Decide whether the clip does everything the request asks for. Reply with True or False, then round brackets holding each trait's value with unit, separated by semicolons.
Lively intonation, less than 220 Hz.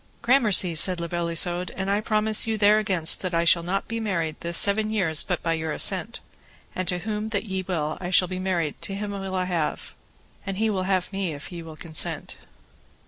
False (3.2 semitones; 185 Hz)